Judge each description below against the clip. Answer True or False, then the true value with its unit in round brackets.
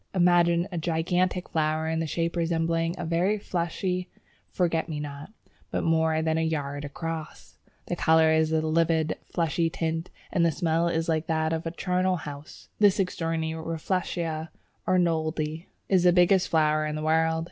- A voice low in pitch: False (165 Hz)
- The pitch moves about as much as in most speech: False (1.5 semitones)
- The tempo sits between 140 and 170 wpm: True (160 wpm)